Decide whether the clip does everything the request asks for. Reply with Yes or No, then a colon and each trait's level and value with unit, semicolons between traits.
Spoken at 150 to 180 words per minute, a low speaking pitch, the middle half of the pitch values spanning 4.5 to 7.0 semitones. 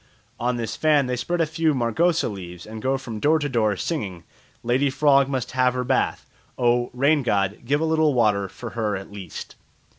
No: average, 200 wpm; low, 125 Hz; average, 5.1 semitones